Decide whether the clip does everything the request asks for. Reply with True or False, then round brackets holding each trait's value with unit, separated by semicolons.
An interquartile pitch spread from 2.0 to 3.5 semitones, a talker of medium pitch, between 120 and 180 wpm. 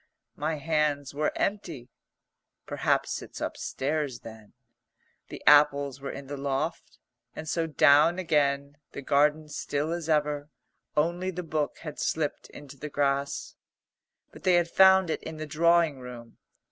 True (2.5 semitones; 150 Hz; 145 wpm)